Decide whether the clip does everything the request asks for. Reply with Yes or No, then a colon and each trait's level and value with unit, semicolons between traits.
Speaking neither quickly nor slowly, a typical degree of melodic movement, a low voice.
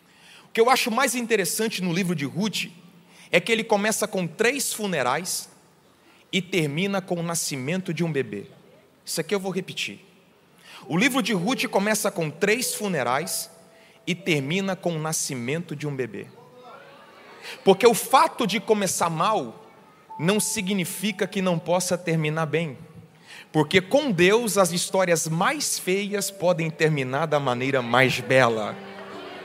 No: average, 150 wpm; average, 4.5 semitones; medium, 185 Hz